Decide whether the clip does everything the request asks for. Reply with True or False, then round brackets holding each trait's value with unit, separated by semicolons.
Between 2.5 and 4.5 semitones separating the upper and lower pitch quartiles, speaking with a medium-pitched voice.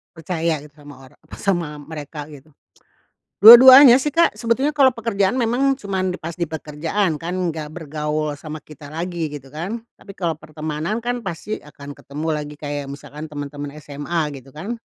False (5.4 semitones; 160 Hz)